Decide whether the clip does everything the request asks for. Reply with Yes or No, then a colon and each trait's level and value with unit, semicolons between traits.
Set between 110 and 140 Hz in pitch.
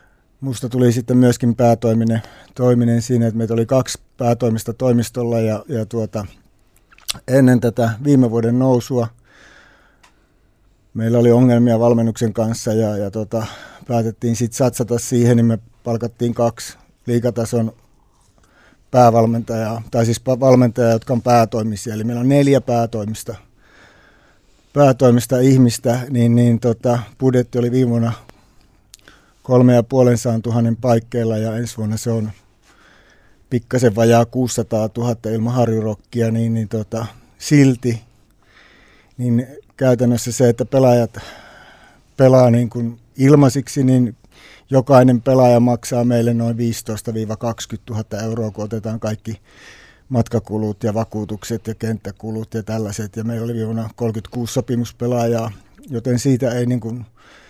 Yes: low, 115 Hz